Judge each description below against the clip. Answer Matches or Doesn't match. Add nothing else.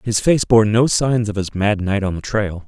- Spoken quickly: Matches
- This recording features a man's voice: Matches